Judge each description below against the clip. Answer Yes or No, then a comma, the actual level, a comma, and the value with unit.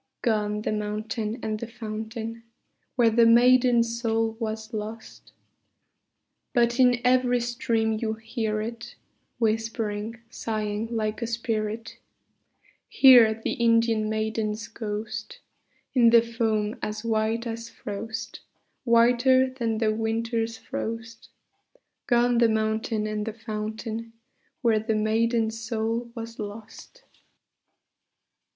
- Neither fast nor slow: No, slow, 110 wpm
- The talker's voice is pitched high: Yes, high, 225 Hz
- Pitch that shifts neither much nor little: No, narrow, 1.3 semitones